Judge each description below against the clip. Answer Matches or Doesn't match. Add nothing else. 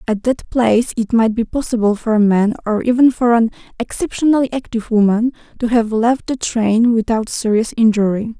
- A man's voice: Doesn't match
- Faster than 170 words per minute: Matches